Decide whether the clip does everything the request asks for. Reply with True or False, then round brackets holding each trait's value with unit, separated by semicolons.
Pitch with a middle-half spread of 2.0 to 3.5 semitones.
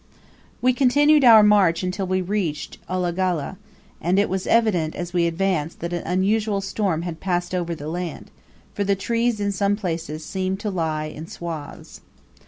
True (3.2 semitones)